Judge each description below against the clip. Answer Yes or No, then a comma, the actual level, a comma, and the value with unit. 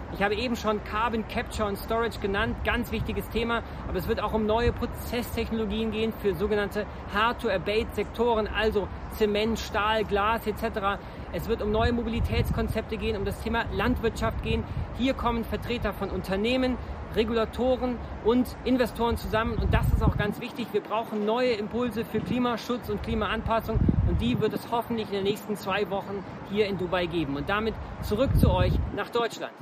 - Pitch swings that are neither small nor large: No, narrow, 2.1 semitones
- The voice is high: Yes, high, 220 Hz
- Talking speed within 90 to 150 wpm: No, average, 170 wpm